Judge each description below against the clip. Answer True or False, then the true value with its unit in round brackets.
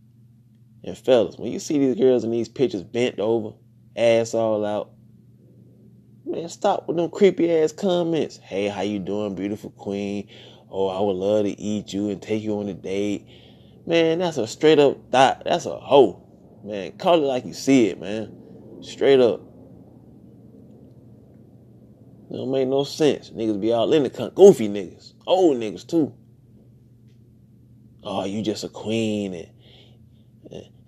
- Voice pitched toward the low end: True (115 Hz)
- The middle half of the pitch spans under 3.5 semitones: True (3.1 semitones)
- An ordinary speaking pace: True (160 wpm)